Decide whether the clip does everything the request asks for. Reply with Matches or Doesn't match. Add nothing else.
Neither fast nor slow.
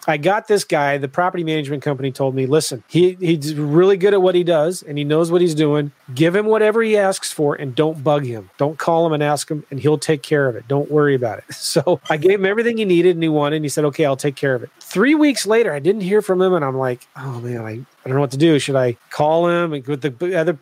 Doesn't match